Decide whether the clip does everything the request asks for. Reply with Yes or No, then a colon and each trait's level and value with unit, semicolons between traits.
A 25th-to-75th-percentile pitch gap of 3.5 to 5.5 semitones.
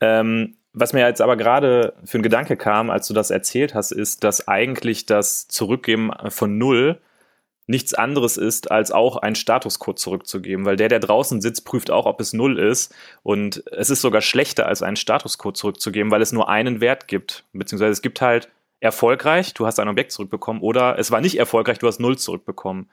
No: average, 2.9 semitones